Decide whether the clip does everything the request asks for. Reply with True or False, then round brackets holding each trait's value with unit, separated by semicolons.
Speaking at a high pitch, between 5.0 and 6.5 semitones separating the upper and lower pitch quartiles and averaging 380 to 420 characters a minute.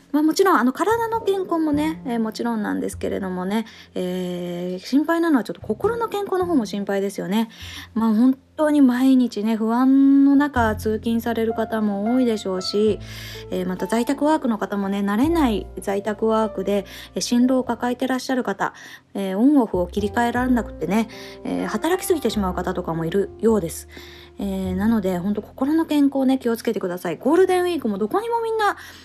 True (225 Hz; 5.9 semitones; 395 characters per minute)